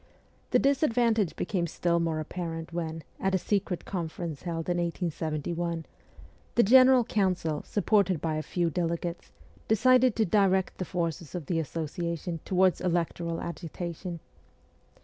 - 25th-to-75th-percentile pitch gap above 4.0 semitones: No, narrow, 2.6 semitones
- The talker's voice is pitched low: No, medium, 175 Hz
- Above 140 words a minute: No, slow, 135 wpm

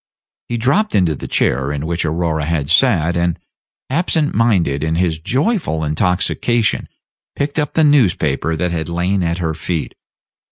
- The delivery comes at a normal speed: Yes, average, 155 wpm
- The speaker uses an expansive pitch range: Yes, wide, 6.9 semitones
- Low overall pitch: Yes, very low, 85 Hz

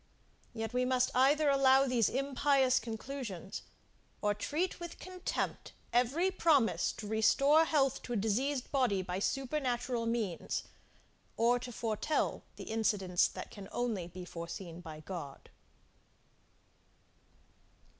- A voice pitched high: Yes, high, 245 Hz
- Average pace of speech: No, slow, 120 wpm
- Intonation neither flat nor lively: Yes, average, 5.0 semitones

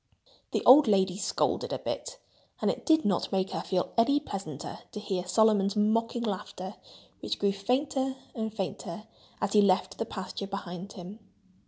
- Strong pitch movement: No, average, 3.2 semitones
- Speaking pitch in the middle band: No, high, 205 Hz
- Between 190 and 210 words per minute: No, average, 165 wpm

